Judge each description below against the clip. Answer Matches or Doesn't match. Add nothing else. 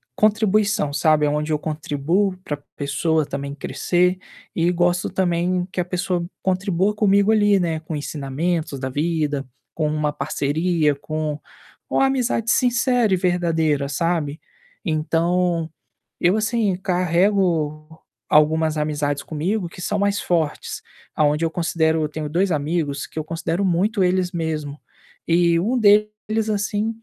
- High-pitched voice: Doesn't match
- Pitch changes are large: Doesn't match